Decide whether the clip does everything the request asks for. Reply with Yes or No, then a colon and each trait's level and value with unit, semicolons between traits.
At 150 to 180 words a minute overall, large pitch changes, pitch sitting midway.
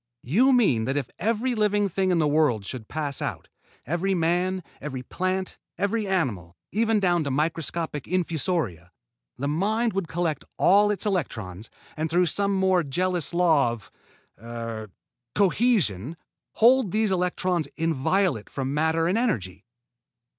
No: average, 140 wpm; wide, 5.9 semitones; medium, 170 Hz